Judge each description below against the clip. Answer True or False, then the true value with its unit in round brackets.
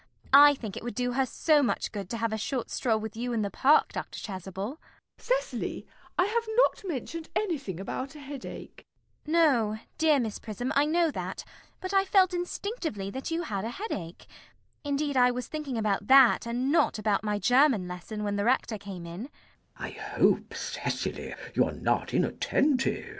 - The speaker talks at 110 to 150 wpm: False (170 wpm)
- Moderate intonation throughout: False (6.3 semitones)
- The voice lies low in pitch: False (250 Hz)